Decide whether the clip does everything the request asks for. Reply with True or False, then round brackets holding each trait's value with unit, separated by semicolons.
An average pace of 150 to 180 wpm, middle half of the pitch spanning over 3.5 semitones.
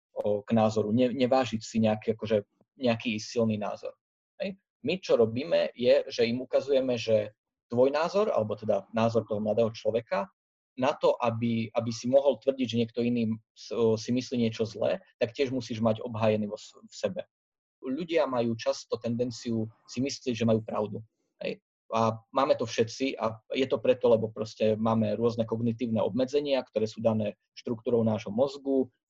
False (160 wpm; 2.7 semitones)